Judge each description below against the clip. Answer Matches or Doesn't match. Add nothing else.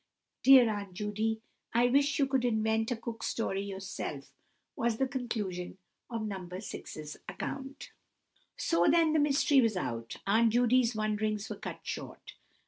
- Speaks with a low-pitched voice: Doesn't match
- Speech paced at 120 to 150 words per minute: Matches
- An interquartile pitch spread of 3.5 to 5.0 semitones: Matches